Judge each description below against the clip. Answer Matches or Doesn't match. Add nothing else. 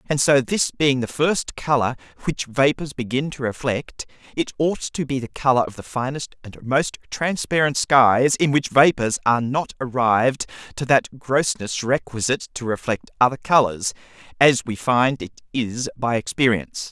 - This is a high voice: Doesn't match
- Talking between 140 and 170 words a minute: Matches